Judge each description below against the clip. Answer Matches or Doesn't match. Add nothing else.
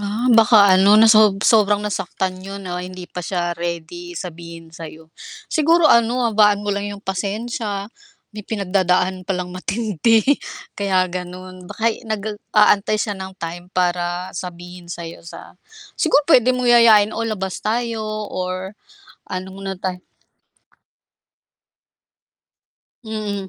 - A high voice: Matches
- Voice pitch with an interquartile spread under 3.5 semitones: Matches